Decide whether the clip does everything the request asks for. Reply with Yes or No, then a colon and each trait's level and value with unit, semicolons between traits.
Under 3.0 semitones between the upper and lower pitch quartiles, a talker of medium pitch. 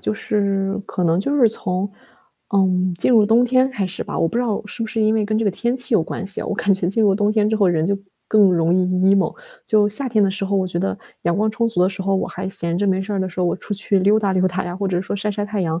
No: narrow, 2.6 semitones; high, 200 Hz